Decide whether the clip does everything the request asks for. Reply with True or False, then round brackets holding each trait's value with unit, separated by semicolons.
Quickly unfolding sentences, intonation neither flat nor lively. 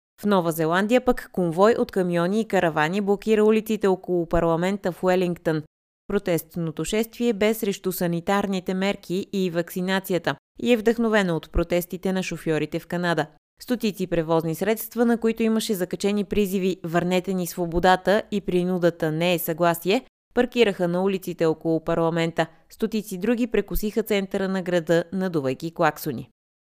False (135 wpm; 3.4 semitones)